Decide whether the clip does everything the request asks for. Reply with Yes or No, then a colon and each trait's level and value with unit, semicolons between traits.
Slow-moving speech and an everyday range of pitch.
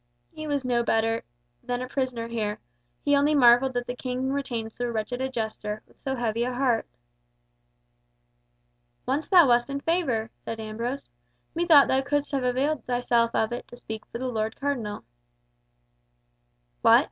No: average, 160 wpm; average, 3.1 semitones